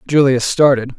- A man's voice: Yes, male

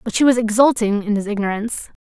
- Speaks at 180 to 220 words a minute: Yes, fast, 205 wpm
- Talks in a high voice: Yes, high, 220 Hz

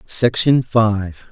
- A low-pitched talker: Yes, low, 110 Hz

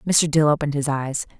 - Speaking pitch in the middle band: Yes, medium, 150 Hz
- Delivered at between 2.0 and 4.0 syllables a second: No, 6.0 syllables/s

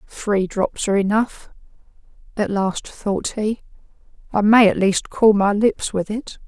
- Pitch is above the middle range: Yes, high, 210 Hz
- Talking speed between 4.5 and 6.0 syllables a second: No, 4.0 syllables/s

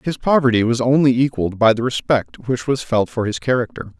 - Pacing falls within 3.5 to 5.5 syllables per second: No, 5.7 syllables/s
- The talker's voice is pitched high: No, low, 125 Hz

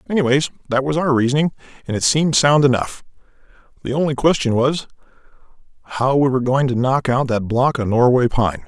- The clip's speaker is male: Yes, male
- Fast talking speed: No, average, 180 wpm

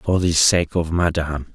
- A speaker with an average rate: Yes, average, 195 wpm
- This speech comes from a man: Yes, male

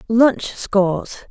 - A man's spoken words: No, female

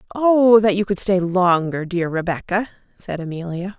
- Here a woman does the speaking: Yes, female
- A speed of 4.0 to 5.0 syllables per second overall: Yes, 4.7 syllables/s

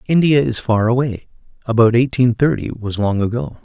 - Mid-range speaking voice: No, low, 120 Hz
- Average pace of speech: Yes, average, 165 wpm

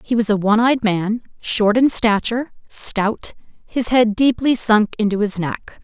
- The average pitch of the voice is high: Yes, high, 220 Hz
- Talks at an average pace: Yes, average, 175 wpm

